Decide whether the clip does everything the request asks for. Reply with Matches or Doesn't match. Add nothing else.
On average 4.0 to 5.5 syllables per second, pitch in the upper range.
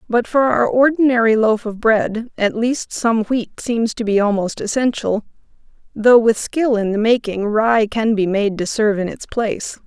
Matches